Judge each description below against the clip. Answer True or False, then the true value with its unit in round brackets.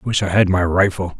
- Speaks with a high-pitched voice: False (95 Hz)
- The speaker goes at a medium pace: False (250 wpm)